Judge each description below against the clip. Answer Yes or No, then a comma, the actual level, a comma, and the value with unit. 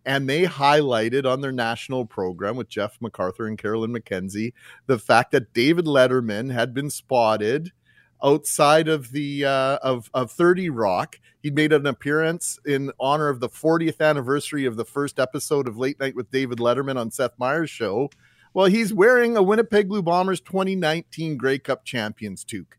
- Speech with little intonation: No, average, 4.0 semitones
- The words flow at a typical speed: Yes, average, 170 wpm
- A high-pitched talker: No, medium, 140 Hz